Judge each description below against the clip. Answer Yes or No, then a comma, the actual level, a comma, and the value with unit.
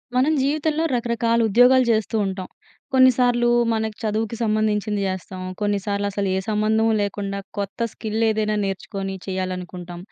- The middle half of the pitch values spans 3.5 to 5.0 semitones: No, average, 2.9 semitones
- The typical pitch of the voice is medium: No, high, 215 Hz